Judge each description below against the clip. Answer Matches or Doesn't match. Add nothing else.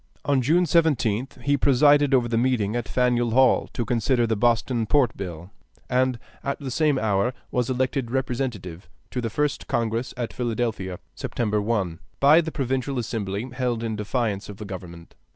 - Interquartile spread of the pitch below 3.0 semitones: Doesn't match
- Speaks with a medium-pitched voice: Doesn't match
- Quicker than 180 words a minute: Doesn't match